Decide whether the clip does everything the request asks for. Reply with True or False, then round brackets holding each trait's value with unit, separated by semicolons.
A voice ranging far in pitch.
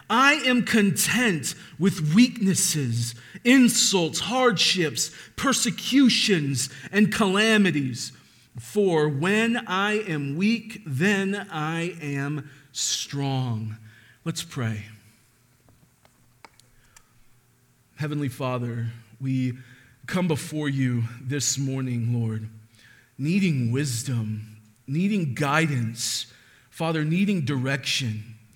True (7.6 semitones)